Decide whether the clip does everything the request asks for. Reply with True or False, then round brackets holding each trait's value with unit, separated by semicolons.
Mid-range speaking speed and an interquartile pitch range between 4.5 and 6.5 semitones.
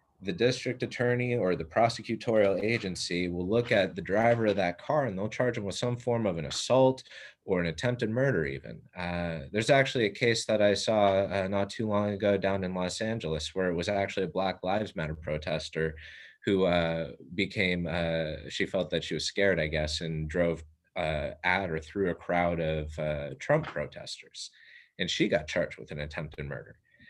True (195 wpm; 5.3 semitones)